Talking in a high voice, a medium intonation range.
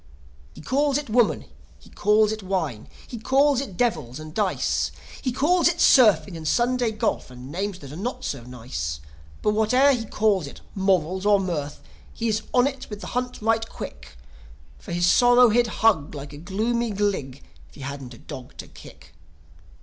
No: high, 205 Hz; wide, 7.7 semitones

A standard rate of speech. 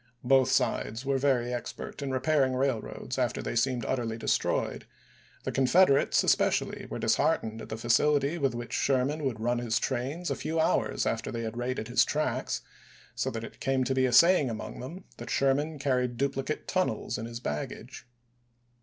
Yes: average, 185 wpm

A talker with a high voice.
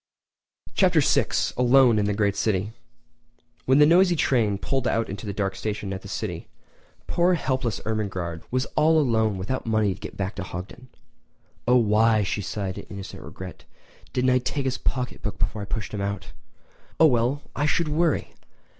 No: low, 110 Hz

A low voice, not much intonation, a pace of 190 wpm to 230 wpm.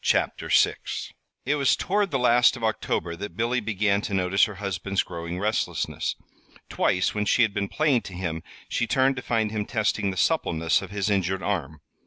No: low, 105 Hz; average, 4.0 semitones; average, 195 wpm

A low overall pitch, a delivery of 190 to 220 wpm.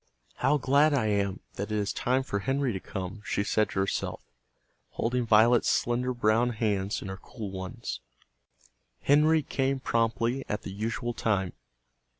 No: low, 115 Hz; average, 155 wpm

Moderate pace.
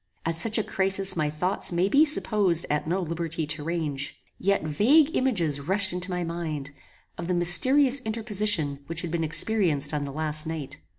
Yes: average, 180 wpm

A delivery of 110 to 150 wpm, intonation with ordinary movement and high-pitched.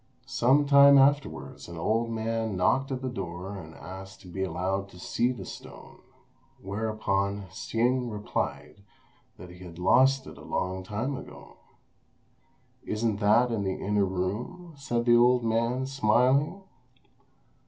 No: average, 145 wpm; average, 4.9 semitones; low, 110 Hz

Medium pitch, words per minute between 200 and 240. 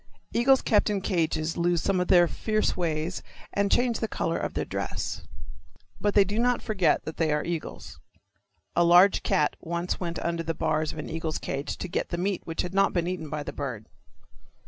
Yes: medium, 175 Hz; fast, 205 wpm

